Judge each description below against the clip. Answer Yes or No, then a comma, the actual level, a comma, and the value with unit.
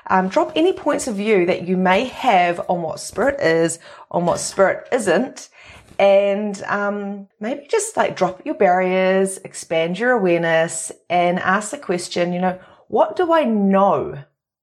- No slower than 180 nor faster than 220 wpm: No, average, 160 wpm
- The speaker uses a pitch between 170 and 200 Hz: Yes, high, 190 Hz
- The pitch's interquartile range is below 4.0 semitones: No, average, 4.8 semitones